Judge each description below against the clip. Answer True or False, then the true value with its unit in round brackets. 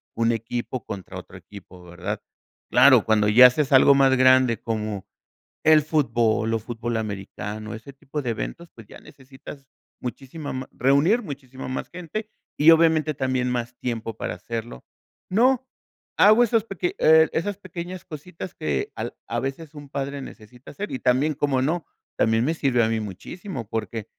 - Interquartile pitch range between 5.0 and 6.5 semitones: True (5.5 semitones)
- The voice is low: True (130 Hz)